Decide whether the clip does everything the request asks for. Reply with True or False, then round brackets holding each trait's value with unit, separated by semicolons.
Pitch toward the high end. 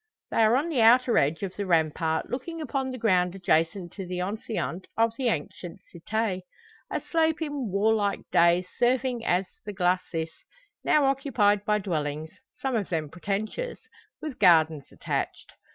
True (205 Hz)